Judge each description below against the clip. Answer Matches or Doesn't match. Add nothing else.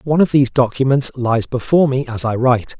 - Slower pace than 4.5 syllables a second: Doesn't match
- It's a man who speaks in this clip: Matches